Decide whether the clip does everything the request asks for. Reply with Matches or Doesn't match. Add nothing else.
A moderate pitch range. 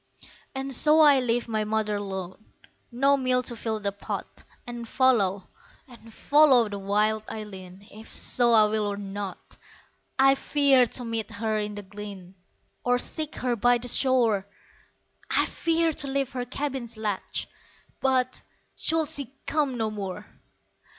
Matches